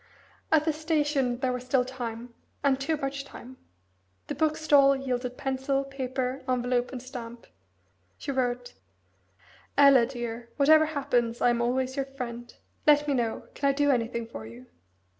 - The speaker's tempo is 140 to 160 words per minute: Yes, average, 155 wpm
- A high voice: Yes, very high, 260 Hz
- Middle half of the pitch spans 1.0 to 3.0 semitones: Yes, narrow, 2.4 semitones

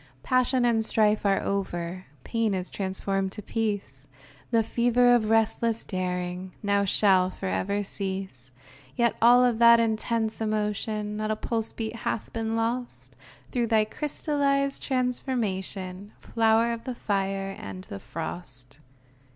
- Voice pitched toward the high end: Yes, high, 215 Hz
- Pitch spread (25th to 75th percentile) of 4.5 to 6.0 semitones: No, average, 3.3 semitones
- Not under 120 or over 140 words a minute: Yes, slow, 135 wpm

